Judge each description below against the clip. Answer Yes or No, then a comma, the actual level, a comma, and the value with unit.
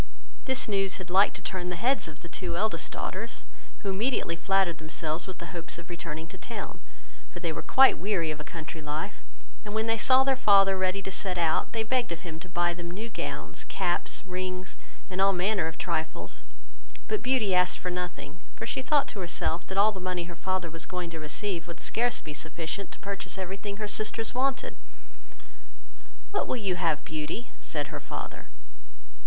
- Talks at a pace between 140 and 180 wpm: No, fast, 205 wpm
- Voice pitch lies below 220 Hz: Yes, medium, 185 Hz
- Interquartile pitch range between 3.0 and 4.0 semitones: Yes, average, 3.6 semitones